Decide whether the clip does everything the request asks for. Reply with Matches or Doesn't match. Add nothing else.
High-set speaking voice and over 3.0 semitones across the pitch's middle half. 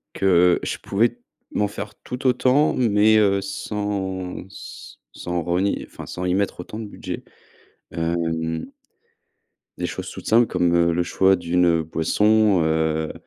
Doesn't match